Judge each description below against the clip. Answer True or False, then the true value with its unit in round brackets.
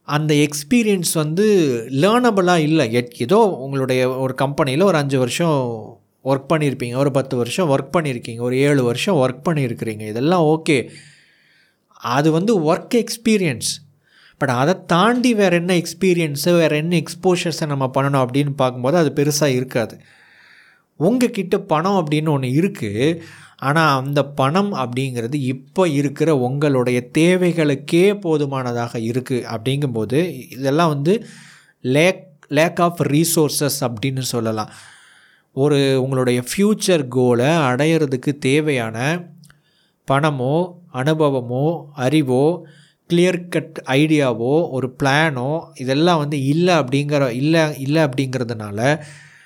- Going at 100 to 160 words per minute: True (110 wpm)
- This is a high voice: False (150 Hz)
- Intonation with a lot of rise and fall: False (4.4 semitones)